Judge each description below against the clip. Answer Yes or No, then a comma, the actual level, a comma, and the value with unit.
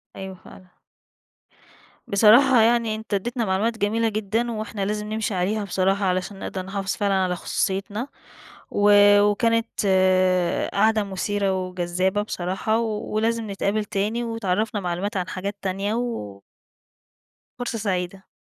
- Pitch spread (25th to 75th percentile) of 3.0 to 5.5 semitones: No, narrow, 2.6 semitones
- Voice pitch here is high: Yes, high, 205 Hz